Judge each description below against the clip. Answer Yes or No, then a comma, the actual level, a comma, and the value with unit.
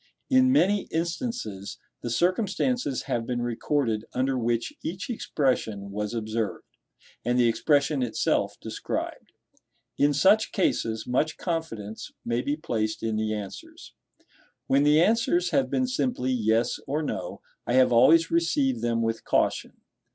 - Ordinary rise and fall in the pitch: No, wide, 6.8 semitones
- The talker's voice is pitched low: Yes, low, 130 Hz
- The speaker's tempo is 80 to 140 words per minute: Yes, slow, 135 wpm